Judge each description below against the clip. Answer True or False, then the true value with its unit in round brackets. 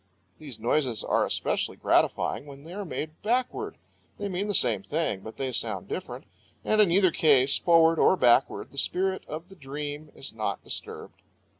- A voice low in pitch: False (155 Hz)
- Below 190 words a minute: True (175 wpm)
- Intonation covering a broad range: True (5.8 semitones)